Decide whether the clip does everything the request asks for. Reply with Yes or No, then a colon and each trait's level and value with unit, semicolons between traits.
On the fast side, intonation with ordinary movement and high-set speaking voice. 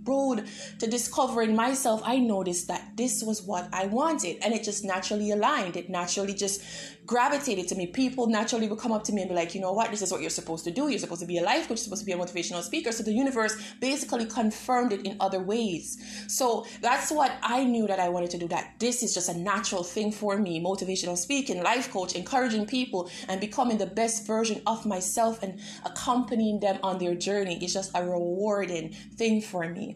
Yes: fast, 220 wpm; average, 3.8 semitones; high, 210 Hz